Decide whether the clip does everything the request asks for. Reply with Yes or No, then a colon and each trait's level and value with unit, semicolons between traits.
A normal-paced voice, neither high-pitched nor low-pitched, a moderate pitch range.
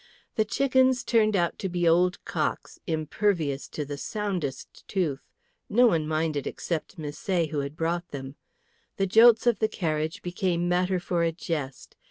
Yes: average, 160 wpm; medium, 175 Hz; average, 4.3 semitones